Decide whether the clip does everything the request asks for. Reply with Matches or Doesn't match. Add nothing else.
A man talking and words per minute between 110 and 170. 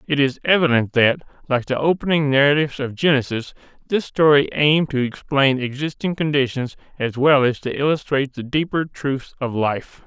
Matches